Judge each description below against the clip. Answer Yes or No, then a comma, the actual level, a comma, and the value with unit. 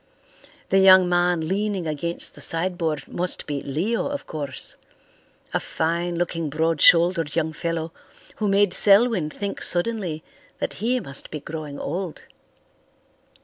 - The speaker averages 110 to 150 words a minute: Yes, slow, 135 wpm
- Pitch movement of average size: Yes, average, 3.3 semitones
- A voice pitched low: No, medium, 170 Hz